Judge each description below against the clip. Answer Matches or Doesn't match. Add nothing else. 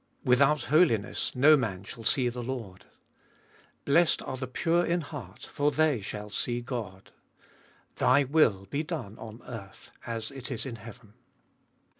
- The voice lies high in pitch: Doesn't match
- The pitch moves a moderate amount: Matches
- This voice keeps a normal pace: Matches